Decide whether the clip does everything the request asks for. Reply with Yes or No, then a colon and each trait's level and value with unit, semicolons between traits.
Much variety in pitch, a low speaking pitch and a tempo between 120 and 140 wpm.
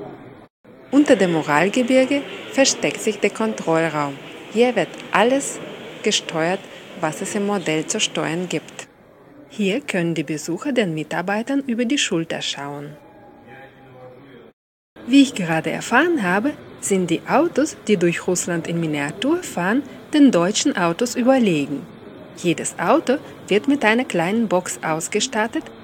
No: wide, 7.3 semitones; high, 195 Hz; slow, 125 wpm